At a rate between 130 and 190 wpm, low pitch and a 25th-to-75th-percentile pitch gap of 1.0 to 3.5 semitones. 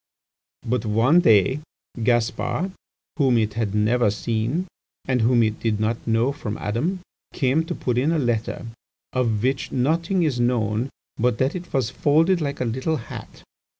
No: average, 160 wpm; low, 125 Hz; average, 4.1 semitones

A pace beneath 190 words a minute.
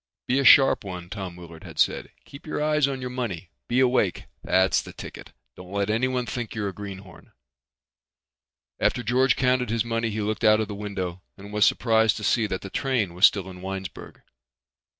No: average, 195 wpm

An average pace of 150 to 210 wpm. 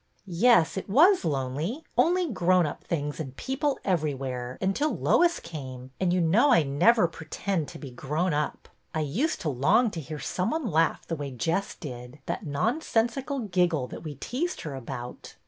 Yes: average, 175 wpm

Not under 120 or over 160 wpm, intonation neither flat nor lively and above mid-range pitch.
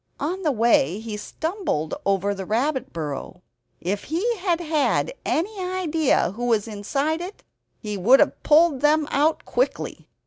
No: average, 150 wpm; wide, 8.1 semitones; very high, 285 Hz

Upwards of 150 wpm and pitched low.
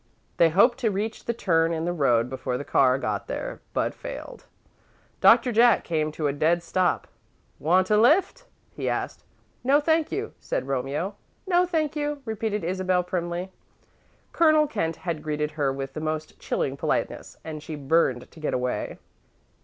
No: average, 170 wpm; medium, 175 Hz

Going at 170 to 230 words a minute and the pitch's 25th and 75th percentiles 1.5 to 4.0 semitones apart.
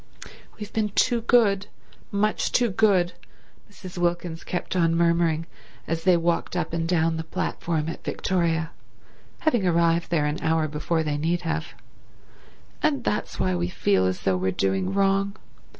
No: average, 150 wpm; average, 3.2 semitones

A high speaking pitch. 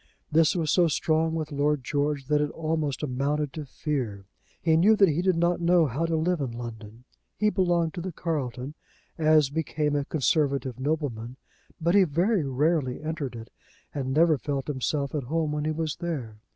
No: medium, 150 Hz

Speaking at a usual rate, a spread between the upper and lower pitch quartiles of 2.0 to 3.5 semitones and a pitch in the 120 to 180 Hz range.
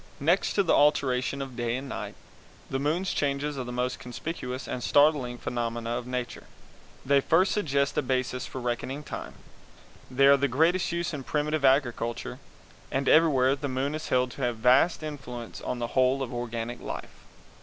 Yes: average, 180 wpm; average, 2.9 semitones; low, 135 Hz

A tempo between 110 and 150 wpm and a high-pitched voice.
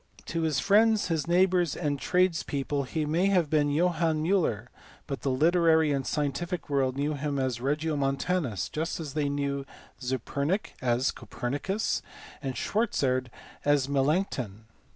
No: average, 140 wpm; medium, 150 Hz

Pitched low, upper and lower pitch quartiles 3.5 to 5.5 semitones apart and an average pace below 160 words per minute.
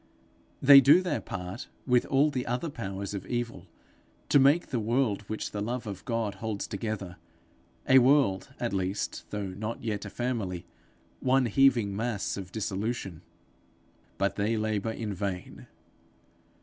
Yes: low, 110 Hz; average, 4.0 semitones; average, 150 wpm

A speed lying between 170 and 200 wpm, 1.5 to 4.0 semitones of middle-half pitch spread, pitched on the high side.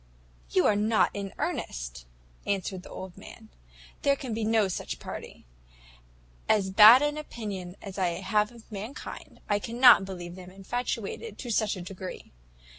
No: average, 155 wpm; average, 3.4 semitones; high, 205 Hz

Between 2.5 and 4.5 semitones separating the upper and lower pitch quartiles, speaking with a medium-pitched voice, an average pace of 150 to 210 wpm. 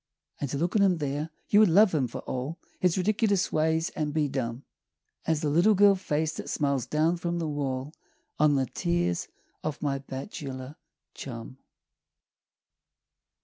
Yes: average, 4.1 semitones; medium, 150 Hz; average, 160 wpm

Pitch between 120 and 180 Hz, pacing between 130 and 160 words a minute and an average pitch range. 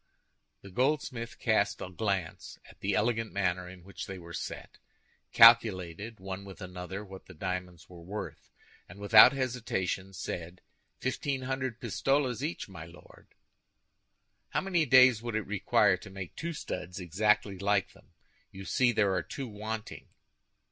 No: low, 100 Hz; average, 150 wpm; average, 4.2 semitones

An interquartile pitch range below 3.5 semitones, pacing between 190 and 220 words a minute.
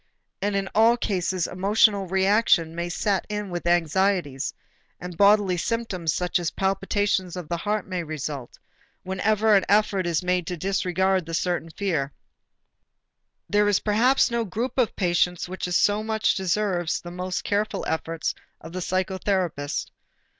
No: average, 2.9 semitones; average, 145 wpm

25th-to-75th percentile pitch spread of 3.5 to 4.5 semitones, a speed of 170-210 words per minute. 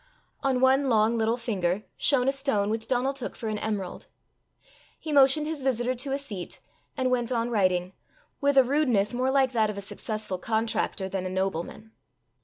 Yes: average, 4.2 semitones; average, 185 wpm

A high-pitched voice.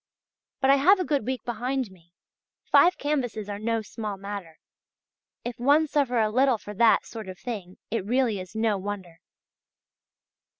Yes: high, 225 Hz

